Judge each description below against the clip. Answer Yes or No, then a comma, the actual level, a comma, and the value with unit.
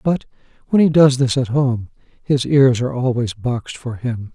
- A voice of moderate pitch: No, low, 130 Hz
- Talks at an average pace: Yes, average, 195 wpm